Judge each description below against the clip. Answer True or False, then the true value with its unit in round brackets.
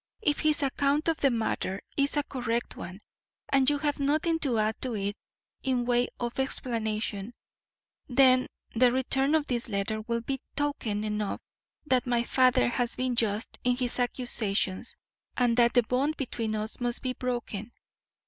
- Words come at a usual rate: True (165 wpm)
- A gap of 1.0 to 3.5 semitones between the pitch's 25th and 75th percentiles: True (3.1 semitones)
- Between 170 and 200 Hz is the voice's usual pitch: False (245 Hz)